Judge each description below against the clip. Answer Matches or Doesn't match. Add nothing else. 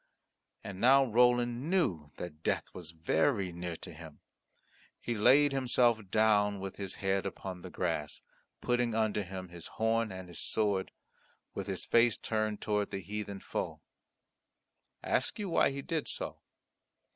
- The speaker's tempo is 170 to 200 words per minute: Doesn't match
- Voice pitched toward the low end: Matches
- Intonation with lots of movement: Doesn't match